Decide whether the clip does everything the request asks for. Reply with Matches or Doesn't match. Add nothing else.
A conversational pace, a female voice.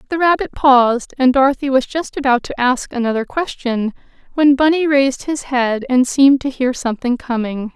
Matches